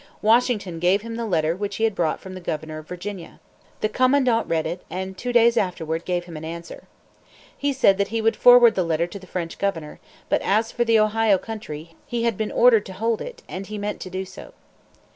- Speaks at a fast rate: Yes, fast, 225 wpm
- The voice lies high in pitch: Yes, high, 200 Hz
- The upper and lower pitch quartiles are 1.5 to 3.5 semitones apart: No, average, 4.7 semitones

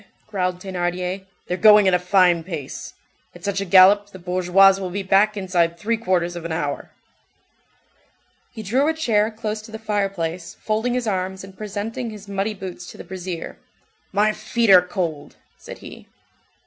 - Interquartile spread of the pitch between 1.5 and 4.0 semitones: Yes, average, 2.9 semitones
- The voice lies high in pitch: Yes, high, 195 Hz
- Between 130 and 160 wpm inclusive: No, average, 175 wpm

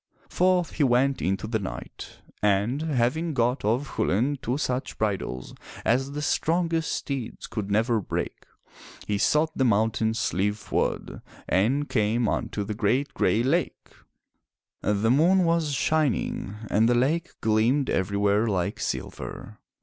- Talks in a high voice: No, low, 120 Hz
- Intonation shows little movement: No, wide, 5.5 semitones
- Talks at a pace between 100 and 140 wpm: Yes, slow, 135 wpm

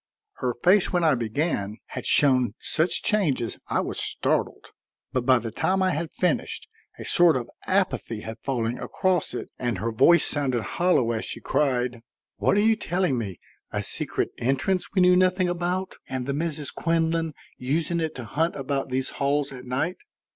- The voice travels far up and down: Yes, wide, 6.0 semitones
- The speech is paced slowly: No, average, 175 wpm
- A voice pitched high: No, medium, 145 Hz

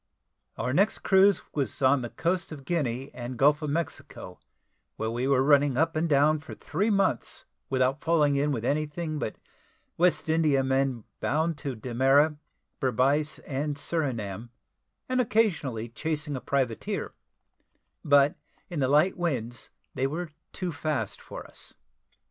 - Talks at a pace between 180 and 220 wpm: No, average, 145 wpm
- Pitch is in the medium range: Yes, medium, 145 Hz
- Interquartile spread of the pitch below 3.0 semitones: No, average, 3.5 semitones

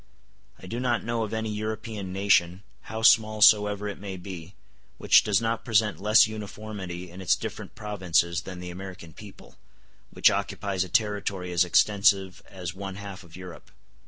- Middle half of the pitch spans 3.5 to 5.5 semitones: No, average, 2.8 semitones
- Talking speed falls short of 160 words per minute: No, average, 165 wpm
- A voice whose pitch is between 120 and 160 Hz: No, low, 100 Hz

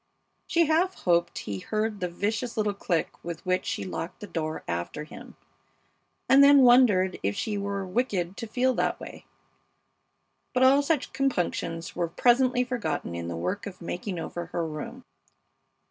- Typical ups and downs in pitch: No, wide, 6.7 semitones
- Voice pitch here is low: No, high, 200 Hz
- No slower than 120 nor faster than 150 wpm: No, average, 160 wpm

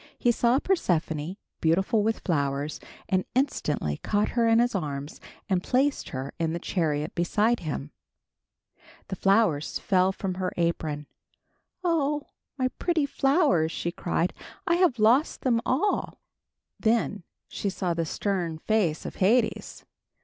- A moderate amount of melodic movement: No, wide, 6.7 semitones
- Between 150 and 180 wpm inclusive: No, slow, 135 wpm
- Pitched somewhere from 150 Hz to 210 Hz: Yes, high, 190 Hz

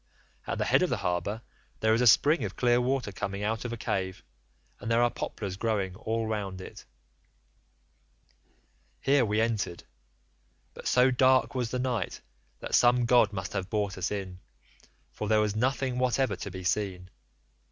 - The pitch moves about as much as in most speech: Yes, average, 4.0 semitones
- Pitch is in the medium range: No, low, 110 Hz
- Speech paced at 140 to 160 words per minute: No, average, 175 wpm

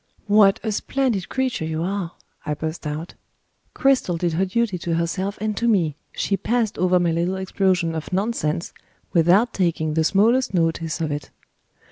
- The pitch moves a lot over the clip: No, average, 4.1 semitones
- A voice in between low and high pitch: Yes, medium, 180 Hz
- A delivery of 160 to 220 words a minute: Yes, average, 165 wpm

